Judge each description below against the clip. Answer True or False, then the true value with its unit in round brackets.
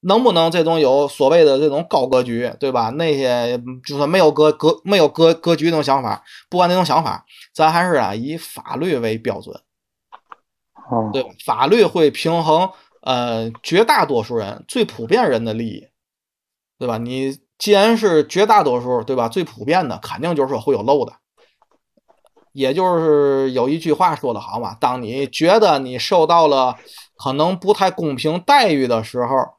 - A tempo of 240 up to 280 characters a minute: True (250 characters per minute)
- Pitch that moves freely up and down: False (4.9 semitones)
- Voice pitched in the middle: True (145 Hz)